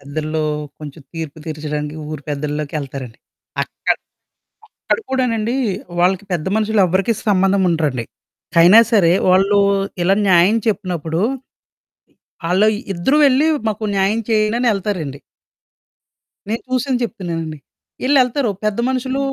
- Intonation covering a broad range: Yes, wide, 6.0 semitones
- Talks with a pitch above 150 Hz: Yes, high, 190 Hz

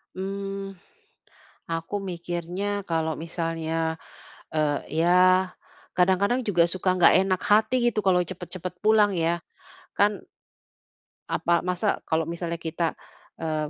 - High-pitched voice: No, medium, 175 Hz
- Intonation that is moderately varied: Yes, average, 3.0 semitones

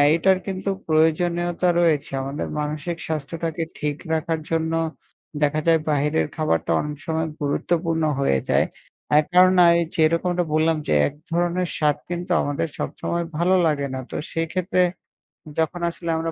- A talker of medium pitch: Yes, medium, 165 Hz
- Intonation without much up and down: Yes, narrow, 2.3 semitones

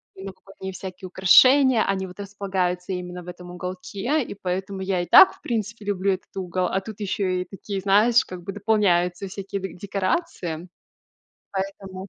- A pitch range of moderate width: No, narrow, 1.9 semitones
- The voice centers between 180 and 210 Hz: Yes, high, 190 Hz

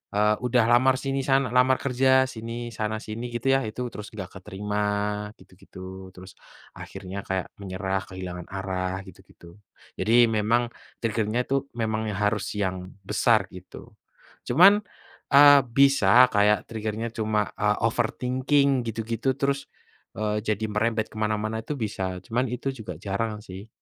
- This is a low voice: Yes, low, 110 Hz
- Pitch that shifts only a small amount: No, average, 3.4 semitones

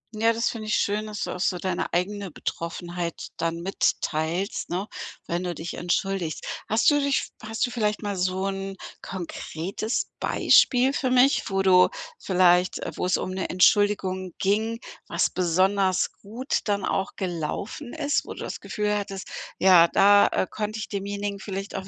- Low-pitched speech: No, high, 195 Hz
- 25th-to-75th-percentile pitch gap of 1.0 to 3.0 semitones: Yes, narrow, 2.6 semitones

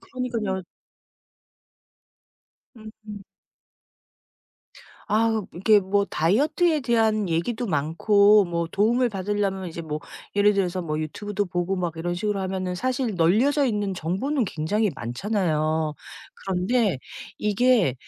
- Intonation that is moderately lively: Yes, average, 4.0 semitones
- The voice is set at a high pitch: Yes, high, 200 Hz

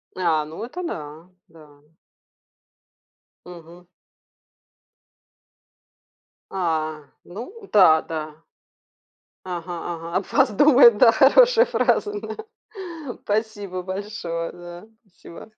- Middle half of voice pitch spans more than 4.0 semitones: Yes, average, 5.0 semitones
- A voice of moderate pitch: Yes, medium, 180 Hz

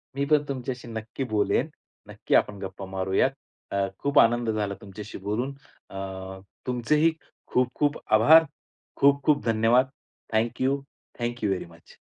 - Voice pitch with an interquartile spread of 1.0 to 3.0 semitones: No, average, 5.0 semitones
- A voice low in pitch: Yes, low, 115 Hz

